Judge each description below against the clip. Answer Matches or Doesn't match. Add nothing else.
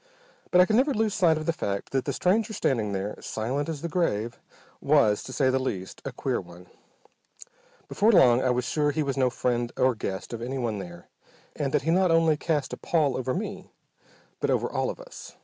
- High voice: Doesn't match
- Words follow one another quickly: Matches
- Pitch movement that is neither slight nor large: Doesn't match